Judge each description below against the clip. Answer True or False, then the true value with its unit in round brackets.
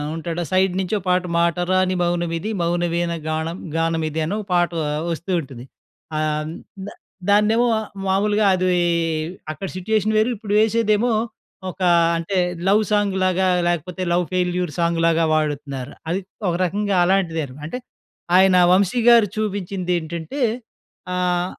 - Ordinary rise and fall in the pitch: True (3.2 semitones)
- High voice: False (180 Hz)